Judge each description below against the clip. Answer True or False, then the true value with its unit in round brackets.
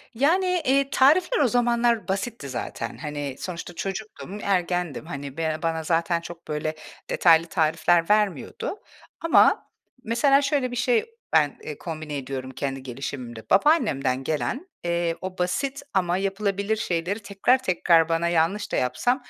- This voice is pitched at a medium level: True (175 Hz)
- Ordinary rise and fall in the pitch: False (7.1 semitones)